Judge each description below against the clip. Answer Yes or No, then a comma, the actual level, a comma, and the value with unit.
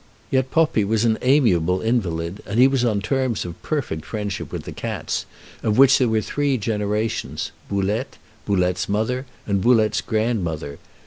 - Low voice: Yes, low, 110 Hz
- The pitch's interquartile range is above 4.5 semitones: No, average, 4.2 semitones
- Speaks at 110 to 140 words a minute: No, average, 155 wpm